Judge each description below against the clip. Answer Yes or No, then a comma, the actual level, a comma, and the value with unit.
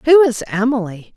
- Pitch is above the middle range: Yes, high, 245 Hz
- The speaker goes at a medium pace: Yes, average, 155 wpm